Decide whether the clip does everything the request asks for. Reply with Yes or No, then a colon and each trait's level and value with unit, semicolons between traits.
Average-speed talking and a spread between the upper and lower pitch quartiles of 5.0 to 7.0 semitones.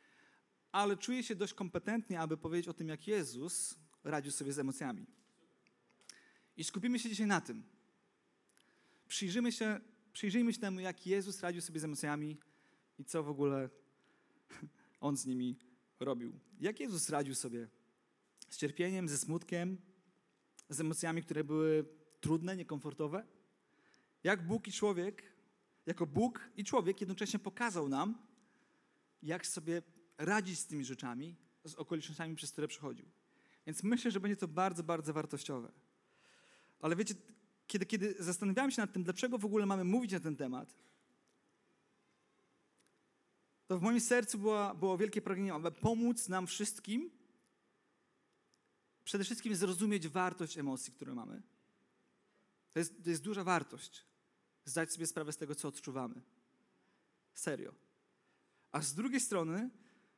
Yes: average, 135 wpm; wide, 5.4 semitones